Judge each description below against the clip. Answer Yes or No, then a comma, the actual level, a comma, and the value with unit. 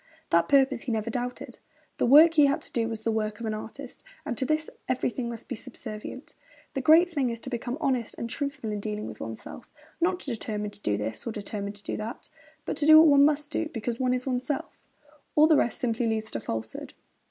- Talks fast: Yes, fast, 230 wpm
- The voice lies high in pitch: Yes, high, 245 Hz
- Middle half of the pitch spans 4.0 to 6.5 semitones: Yes, average, 4.4 semitones